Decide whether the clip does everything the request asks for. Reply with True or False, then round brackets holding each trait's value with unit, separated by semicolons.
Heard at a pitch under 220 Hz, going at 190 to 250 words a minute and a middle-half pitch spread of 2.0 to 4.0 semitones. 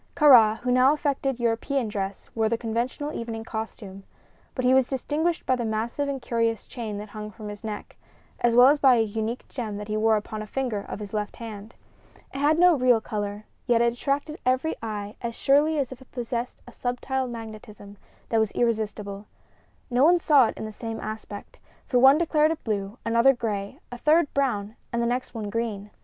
False (235 Hz; 205 wpm; 3.6 semitones)